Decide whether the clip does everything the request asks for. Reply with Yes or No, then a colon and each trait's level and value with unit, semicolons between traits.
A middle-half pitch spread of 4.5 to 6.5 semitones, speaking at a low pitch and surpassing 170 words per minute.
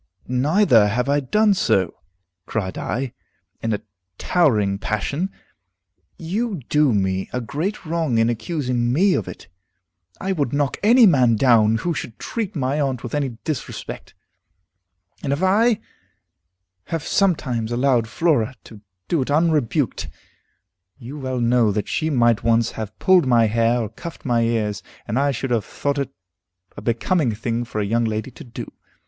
No: wide, 5.4 semitones; low, 125 Hz; average, 160 wpm